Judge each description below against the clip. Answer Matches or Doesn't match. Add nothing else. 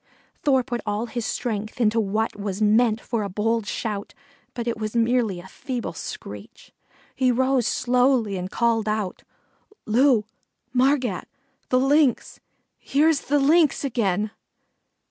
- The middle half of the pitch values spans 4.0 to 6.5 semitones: Doesn't match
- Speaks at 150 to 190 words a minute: Doesn't match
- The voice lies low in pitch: Doesn't match